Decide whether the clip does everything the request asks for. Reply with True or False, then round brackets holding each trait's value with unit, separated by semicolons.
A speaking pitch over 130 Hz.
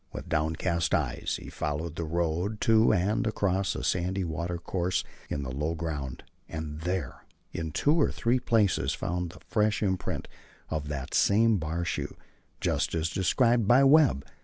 False (85 Hz)